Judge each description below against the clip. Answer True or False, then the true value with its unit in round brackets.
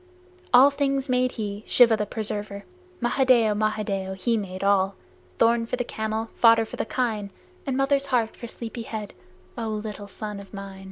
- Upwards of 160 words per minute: True (170 wpm)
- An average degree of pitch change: True (3.1 semitones)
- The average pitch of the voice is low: False (220 Hz)